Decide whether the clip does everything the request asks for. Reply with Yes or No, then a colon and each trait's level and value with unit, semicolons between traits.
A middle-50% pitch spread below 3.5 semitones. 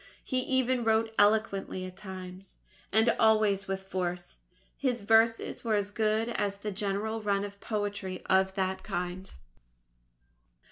Yes: narrow, 2.6 semitones